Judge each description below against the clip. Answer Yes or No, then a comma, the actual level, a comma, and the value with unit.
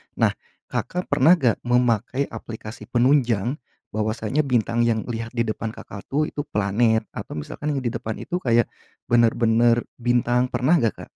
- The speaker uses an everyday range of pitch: No, narrow, 2.2 semitones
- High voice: No, low, 120 Hz